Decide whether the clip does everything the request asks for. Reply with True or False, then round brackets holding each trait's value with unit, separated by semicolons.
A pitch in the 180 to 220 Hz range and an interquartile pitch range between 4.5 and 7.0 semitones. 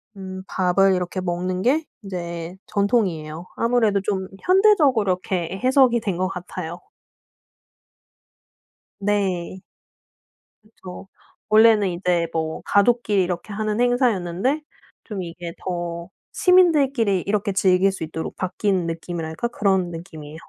False (190 Hz; 3.8 semitones)